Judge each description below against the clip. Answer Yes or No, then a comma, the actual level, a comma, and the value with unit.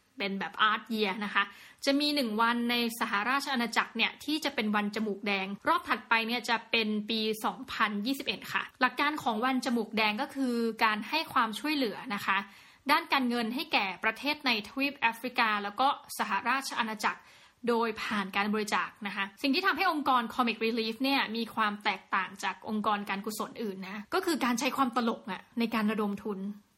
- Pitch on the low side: No, high, 230 Hz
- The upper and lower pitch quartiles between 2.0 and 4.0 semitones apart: Yes, average, 3.7 semitones